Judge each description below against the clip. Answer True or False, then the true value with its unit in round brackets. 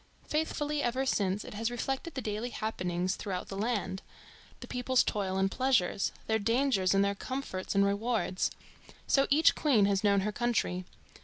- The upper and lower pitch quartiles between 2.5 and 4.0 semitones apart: False (4.7 semitones)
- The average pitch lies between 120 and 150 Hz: False (215 Hz)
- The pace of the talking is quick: False (170 wpm)